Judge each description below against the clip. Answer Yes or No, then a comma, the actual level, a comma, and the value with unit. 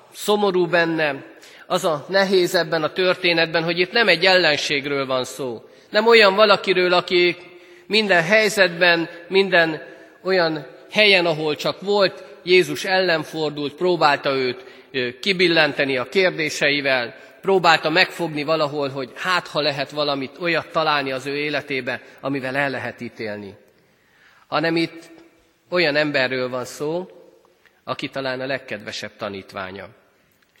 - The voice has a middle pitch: Yes, medium, 165 Hz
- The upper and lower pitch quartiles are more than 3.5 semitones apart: Yes, average, 4.5 semitones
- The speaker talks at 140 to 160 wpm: No, average, 125 wpm